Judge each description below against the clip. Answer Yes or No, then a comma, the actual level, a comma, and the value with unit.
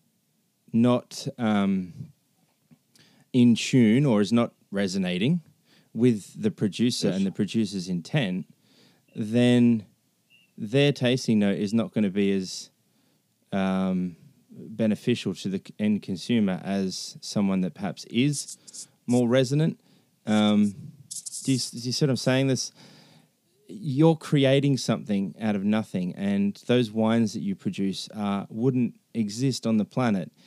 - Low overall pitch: Yes, low, 120 Hz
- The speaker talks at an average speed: No, slow, 130 wpm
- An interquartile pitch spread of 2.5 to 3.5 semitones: No, average, 5.2 semitones